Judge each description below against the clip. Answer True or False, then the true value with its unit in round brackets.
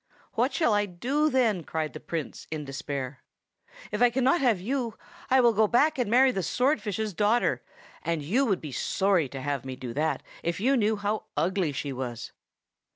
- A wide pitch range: True (7.9 semitones)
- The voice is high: True (205 Hz)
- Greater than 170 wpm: True (190 wpm)